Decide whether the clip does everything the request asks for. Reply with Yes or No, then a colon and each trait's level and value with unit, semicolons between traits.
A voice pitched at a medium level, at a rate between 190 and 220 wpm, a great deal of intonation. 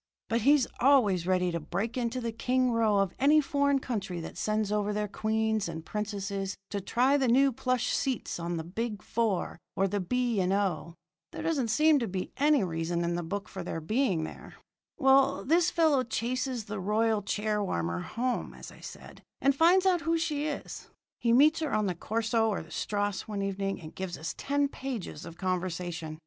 No: high, 215 Hz; average, 200 wpm; wide, 5.7 semitones